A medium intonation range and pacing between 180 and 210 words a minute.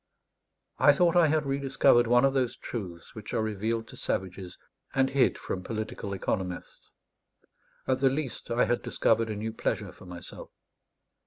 No: average, 4.7 semitones; average, 160 wpm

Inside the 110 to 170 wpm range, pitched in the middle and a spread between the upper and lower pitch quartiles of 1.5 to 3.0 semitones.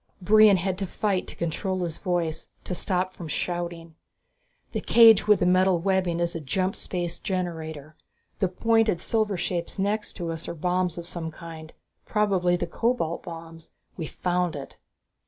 Yes: average, 165 wpm; medium, 180 Hz; narrow, 2.4 semitones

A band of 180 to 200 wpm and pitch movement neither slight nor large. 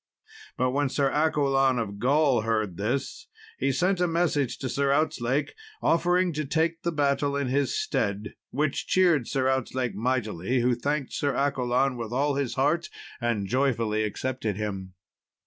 No: average, 155 wpm; average, 3.6 semitones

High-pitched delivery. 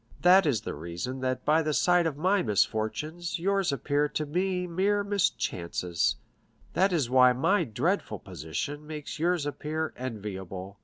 No: medium, 150 Hz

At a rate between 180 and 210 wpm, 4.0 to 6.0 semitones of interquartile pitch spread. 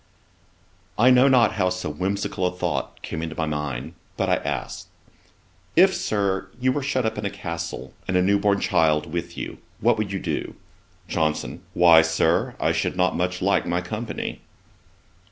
No: average, 170 wpm; average, 4.3 semitones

